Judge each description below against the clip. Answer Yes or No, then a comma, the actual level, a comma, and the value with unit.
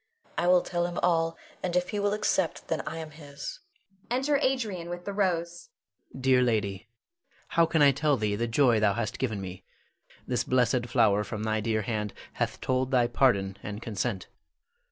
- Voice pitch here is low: Yes, low, 130 Hz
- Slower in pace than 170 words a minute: No, average, 185 wpm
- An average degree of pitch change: No, wide, 7.9 semitones